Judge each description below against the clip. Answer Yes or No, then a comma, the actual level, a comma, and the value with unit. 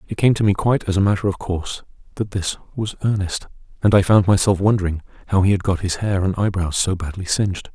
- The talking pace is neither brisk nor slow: No, fast, 235 wpm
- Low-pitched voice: Yes, very low, 95 Hz